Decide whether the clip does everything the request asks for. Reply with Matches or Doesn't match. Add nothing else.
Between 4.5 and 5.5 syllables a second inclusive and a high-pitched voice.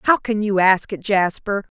Matches